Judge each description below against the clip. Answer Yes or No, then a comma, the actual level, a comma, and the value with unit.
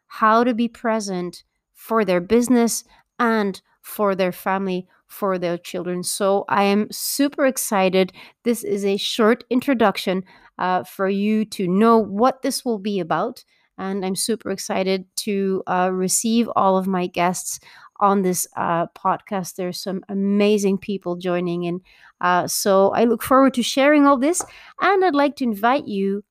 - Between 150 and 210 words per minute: Yes, average, 160 wpm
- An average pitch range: Yes, average, 3.7 semitones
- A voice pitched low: No, high, 200 Hz